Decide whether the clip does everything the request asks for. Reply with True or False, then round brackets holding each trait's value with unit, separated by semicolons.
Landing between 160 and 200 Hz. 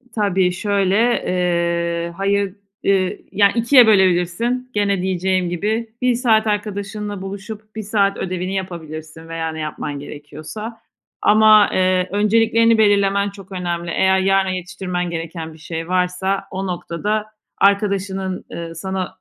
True (190 Hz)